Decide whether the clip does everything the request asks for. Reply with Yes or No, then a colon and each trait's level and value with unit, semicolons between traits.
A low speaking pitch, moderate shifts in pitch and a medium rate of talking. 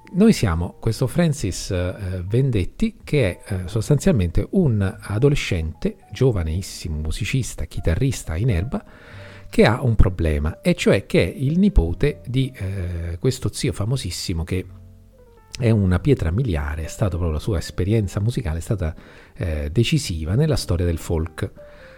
No: low, 100 Hz; wide, 6.5 semitones; average, 140 wpm